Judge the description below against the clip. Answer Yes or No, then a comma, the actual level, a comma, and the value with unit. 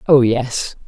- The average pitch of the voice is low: Yes, low, 125 Hz